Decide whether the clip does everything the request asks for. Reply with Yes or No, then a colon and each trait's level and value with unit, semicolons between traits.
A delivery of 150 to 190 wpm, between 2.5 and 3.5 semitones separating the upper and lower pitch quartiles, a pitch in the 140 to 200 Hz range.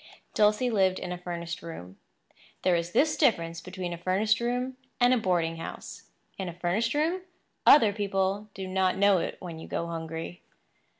No: average, 175 wpm; average, 3.9 semitones; medium, 185 Hz